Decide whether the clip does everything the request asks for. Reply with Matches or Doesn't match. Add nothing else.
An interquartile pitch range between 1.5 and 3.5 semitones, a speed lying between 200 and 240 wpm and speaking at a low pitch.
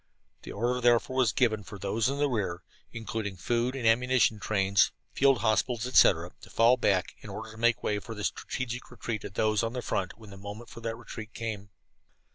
Matches